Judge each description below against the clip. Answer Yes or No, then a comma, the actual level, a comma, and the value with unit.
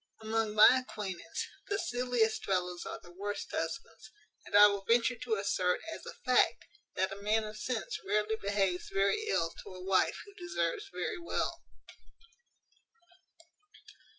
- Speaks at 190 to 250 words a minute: No, average, 150 wpm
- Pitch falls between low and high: No, high, 215 Hz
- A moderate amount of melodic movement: Yes, average, 4.0 semitones